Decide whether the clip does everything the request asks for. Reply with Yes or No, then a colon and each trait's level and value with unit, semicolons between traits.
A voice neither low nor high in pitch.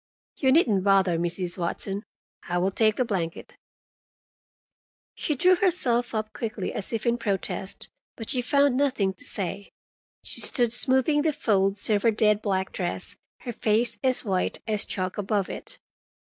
No: high, 215 Hz